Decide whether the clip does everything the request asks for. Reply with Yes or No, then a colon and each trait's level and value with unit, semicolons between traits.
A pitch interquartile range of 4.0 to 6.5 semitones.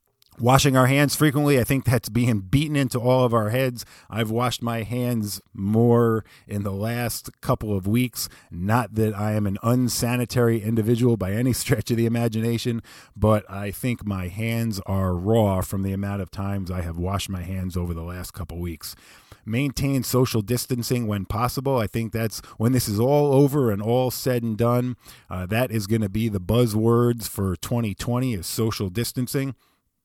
No: average, 3.3 semitones